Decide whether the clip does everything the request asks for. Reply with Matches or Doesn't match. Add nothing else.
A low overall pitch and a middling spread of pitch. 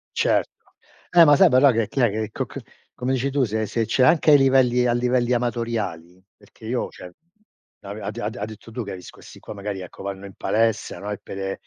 Matches